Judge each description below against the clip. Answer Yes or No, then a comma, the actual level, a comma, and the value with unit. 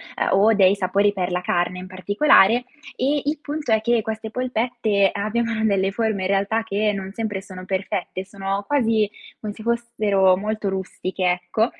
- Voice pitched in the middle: No, high, 205 Hz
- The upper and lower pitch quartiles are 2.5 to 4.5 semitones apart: Yes, average, 2.8 semitones